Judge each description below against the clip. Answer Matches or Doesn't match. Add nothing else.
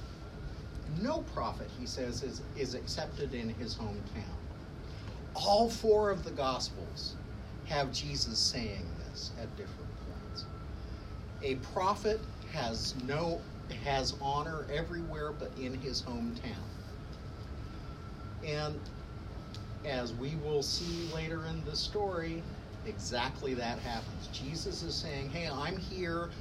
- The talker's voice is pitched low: Matches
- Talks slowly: Matches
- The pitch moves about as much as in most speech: Doesn't match